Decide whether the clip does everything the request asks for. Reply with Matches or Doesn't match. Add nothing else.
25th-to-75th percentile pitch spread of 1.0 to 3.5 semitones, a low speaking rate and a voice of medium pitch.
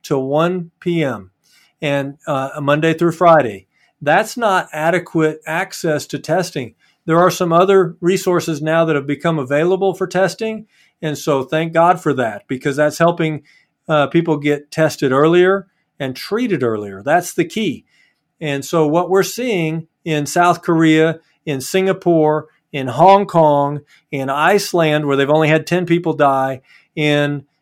Doesn't match